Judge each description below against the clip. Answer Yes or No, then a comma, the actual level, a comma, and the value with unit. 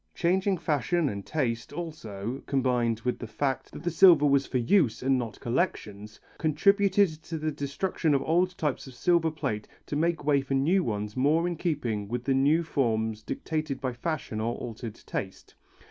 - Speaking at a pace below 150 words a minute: No, average, 175 wpm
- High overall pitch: No, medium, 140 Hz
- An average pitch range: No, wide, 5.7 semitones